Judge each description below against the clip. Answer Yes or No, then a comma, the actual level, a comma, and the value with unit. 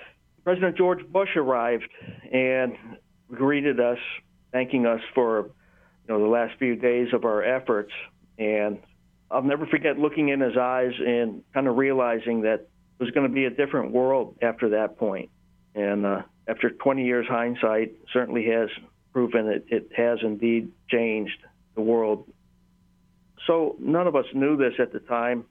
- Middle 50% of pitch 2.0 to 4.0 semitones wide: Yes, average, 2.9 semitones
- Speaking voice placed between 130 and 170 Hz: No, low, 120 Hz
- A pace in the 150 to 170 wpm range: Yes, average, 160 wpm